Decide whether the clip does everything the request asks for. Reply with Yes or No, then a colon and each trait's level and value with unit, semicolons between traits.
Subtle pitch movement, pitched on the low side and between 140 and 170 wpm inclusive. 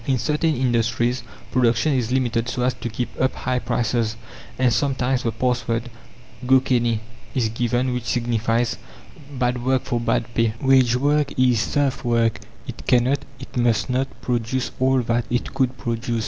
Yes: narrow, 1.8 semitones; low, 125 Hz; average, 165 wpm